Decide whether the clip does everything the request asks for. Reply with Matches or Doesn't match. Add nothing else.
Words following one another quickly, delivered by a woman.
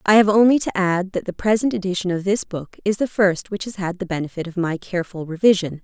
Matches